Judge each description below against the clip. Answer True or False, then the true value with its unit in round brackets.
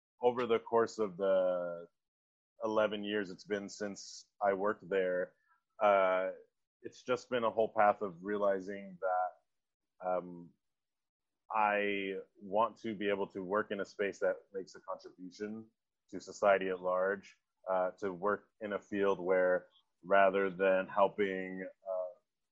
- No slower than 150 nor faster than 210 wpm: False (140 wpm)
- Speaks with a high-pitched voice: False (100 Hz)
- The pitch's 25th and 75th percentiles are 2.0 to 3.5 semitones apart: True (2.5 semitones)